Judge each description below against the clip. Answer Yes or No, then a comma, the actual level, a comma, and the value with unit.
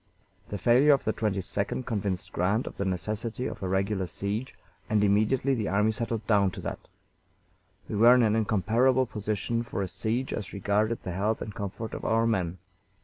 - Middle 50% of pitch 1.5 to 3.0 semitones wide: Yes, narrow, 2.5 semitones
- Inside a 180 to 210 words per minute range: Yes, average, 185 wpm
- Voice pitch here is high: No, low, 105 Hz